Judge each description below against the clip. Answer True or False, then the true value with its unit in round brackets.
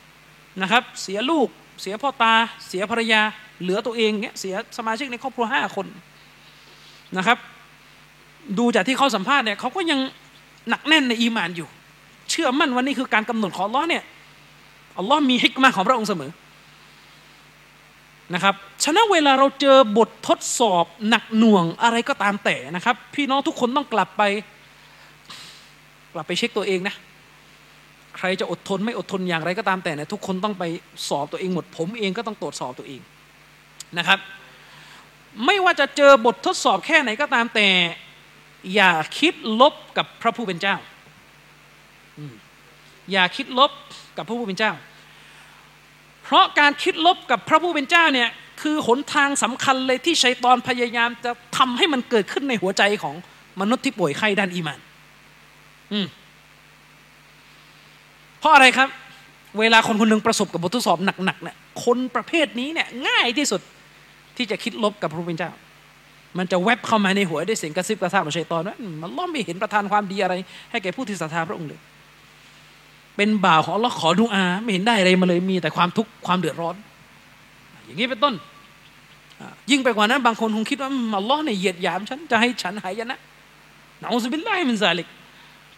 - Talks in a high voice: True (220 Hz)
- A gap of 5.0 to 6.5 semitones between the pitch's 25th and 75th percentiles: True (5.5 semitones)